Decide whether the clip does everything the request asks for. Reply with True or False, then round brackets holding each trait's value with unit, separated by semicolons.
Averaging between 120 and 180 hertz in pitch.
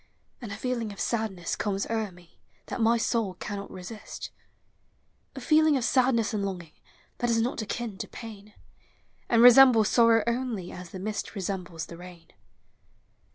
False (215 Hz)